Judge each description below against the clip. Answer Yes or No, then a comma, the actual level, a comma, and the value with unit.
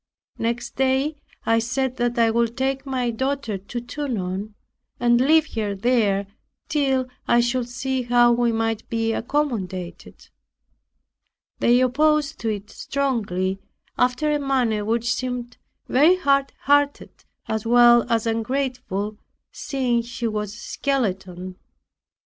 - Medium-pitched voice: No, high, 240 Hz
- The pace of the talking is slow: Yes, slow, 120 wpm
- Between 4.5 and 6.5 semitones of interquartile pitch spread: No, average, 3.2 semitones